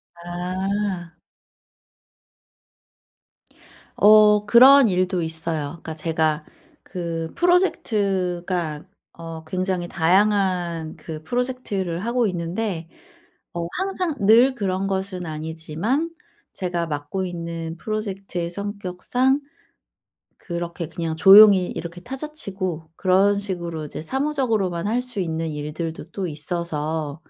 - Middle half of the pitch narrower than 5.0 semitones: Yes, average, 3.9 semitones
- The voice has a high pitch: No, medium, 180 Hz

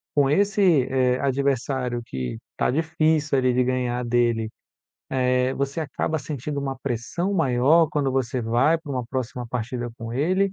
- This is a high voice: No, low, 130 Hz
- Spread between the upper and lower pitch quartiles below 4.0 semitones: Yes, average, 3.5 semitones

